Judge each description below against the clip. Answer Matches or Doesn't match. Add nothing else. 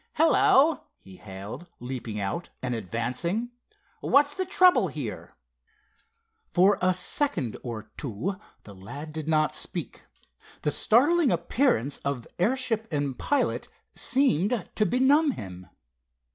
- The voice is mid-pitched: Matches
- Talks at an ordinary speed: Doesn't match